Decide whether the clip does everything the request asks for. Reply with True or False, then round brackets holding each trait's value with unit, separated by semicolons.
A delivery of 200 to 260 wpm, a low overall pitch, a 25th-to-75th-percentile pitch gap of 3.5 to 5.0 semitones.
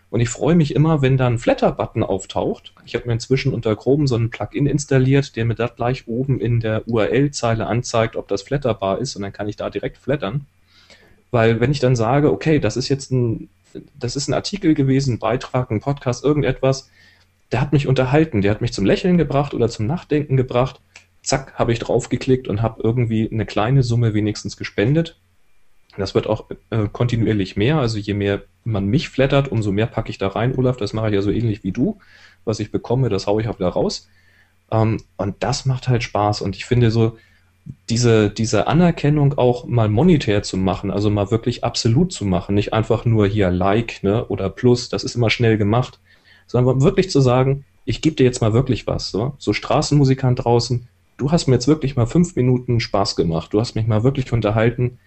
True (205 wpm; 115 Hz; 4.2 semitones)